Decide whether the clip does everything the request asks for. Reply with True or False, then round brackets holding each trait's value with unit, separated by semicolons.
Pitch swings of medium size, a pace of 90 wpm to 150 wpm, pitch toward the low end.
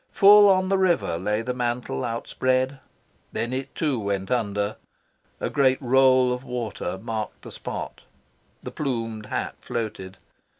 True (3.5 semitones; 140 wpm; 125 Hz)